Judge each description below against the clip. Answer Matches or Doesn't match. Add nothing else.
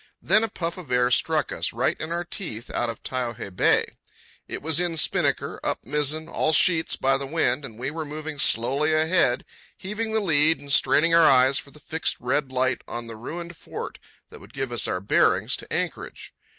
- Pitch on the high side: Doesn't match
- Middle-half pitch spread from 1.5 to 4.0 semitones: Doesn't match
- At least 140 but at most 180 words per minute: Doesn't match